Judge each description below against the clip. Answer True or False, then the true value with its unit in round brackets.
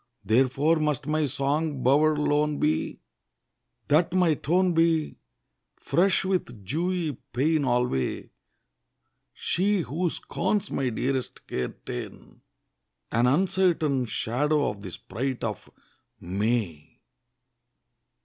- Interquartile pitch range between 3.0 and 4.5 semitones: False (5.0 semitones)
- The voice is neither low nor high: True (145 Hz)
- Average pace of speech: False (100 wpm)